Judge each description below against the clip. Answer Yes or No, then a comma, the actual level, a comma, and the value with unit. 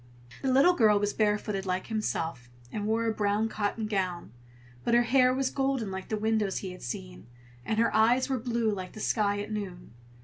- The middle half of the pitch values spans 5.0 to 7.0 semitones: No, average, 3.1 semitones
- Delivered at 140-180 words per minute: No, average, 200 wpm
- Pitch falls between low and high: No, high, 215 Hz